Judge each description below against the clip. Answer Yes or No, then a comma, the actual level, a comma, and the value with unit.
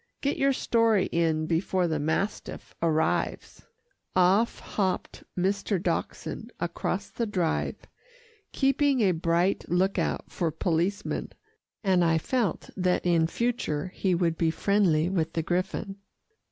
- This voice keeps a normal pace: No, slow, 125 wpm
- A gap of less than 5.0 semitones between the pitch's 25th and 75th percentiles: Yes, average, 3.7 semitones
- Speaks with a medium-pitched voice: Yes, medium, 180 Hz